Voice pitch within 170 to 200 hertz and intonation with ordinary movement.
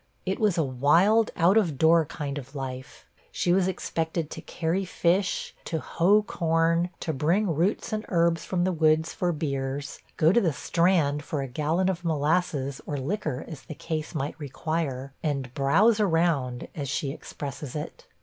No: medium, 160 Hz; average, 3.9 semitones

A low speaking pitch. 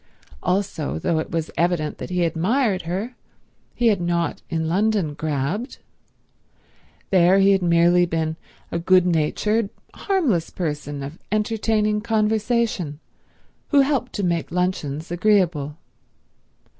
No: medium, 180 Hz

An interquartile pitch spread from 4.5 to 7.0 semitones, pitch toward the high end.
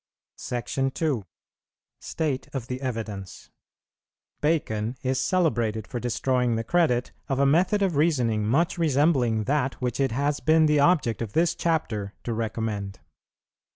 No: average, 5.2 semitones; low, 130 Hz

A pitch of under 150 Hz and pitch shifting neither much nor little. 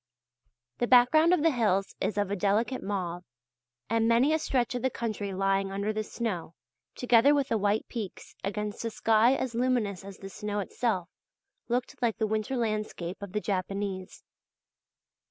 No: high, 215 Hz; average, 3.5 semitones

